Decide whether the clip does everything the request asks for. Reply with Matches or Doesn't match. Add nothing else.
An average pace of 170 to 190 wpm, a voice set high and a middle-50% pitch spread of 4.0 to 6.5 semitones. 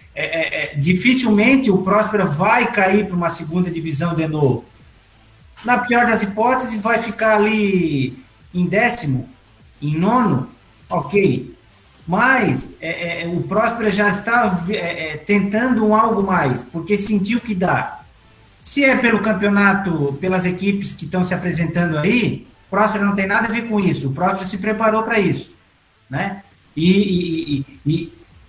Doesn't match